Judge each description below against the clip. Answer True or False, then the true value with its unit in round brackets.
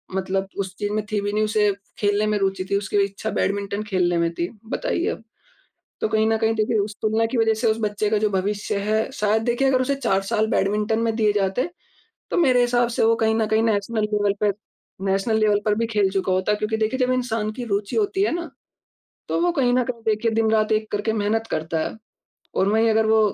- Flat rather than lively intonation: True (1.8 semitones)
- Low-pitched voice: False (215 Hz)